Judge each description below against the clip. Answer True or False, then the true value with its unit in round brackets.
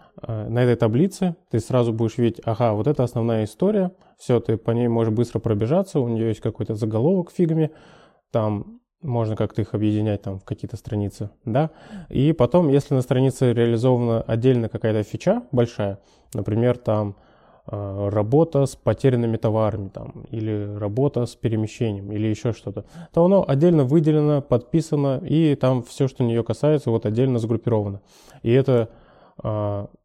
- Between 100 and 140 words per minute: False (150 wpm)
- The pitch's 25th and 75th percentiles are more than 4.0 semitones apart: True (4.6 semitones)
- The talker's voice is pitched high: False (120 Hz)